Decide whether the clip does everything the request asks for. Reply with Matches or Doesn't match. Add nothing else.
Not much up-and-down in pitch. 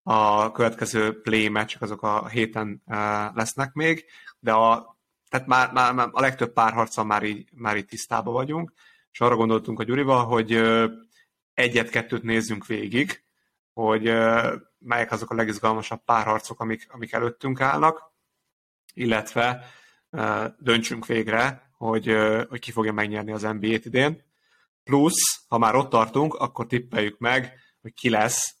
Matches